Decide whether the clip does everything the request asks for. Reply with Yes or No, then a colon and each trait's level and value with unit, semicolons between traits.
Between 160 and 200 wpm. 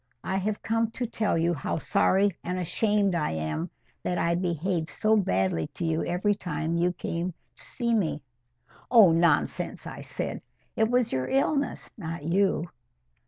Yes: average, 165 wpm